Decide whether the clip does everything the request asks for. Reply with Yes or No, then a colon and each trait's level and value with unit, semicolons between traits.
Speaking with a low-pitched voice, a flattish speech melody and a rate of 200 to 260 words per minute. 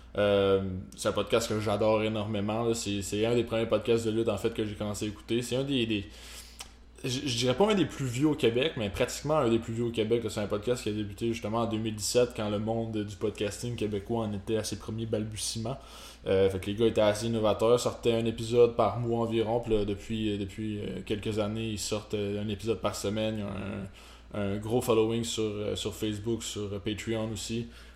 Yes: low, 110 Hz; narrow, 1.9 semitones; fast, 220 wpm